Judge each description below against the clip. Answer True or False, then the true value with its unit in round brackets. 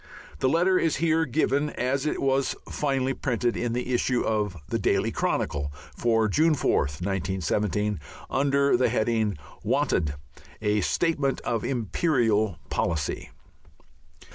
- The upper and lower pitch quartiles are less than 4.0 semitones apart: False (5.0 semitones)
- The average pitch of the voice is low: True (120 Hz)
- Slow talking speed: True (125 wpm)